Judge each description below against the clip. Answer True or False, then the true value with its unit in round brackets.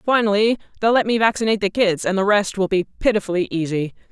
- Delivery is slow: False (205 wpm)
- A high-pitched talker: True (205 Hz)